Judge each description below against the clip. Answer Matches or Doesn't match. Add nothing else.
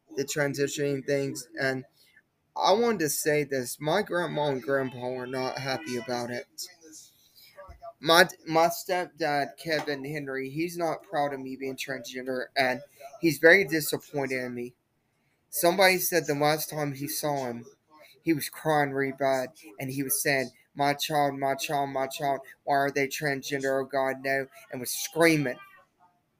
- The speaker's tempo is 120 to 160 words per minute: Matches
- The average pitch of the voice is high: Doesn't match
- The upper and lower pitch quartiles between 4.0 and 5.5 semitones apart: Doesn't match